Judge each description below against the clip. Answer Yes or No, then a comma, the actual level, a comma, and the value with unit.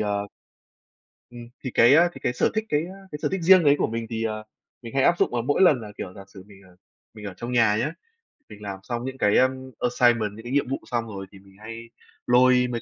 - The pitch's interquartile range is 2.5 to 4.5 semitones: Yes, average, 3.9 semitones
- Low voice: Yes, low, 120 Hz